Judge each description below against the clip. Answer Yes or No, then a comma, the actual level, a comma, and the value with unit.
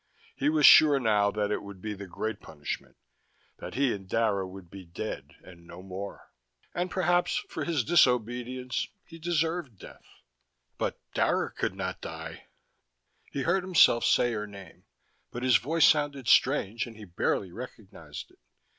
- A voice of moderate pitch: No, low, 115 Hz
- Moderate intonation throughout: No, wide, 6.6 semitones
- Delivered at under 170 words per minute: Yes, average, 160 wpm